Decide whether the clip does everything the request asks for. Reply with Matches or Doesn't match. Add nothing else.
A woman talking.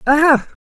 Matches